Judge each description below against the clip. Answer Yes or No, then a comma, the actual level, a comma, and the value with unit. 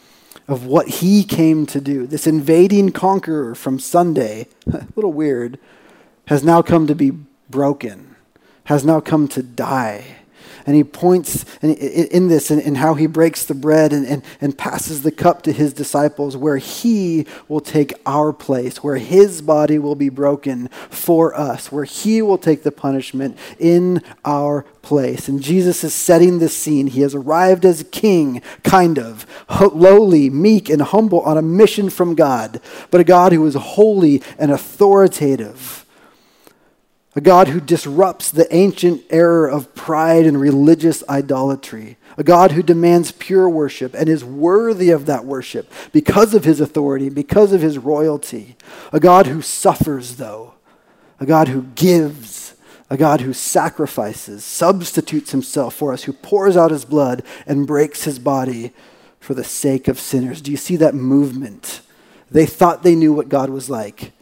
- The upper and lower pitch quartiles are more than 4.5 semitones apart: No, average, 3.6 semitones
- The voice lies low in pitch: No, medium, 150 Hz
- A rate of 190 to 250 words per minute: No, average, 165 wpm